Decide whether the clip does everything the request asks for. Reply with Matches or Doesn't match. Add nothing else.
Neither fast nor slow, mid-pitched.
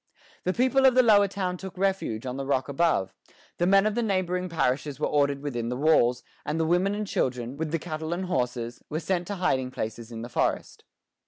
Doesn't match